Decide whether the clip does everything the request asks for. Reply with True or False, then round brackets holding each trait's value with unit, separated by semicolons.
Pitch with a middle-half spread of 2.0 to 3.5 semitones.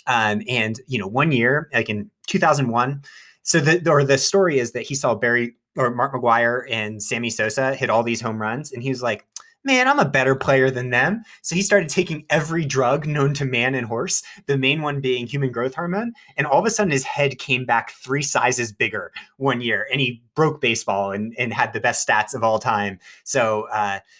False (4.2 semitones)